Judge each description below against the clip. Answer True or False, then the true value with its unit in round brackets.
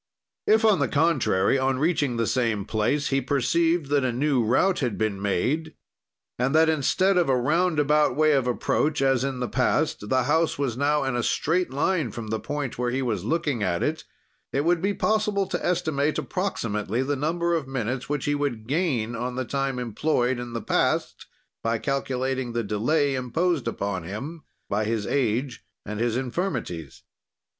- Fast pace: False (180 wpm)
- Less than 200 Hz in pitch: True (135 Hz)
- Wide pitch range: False (4.7 semitones)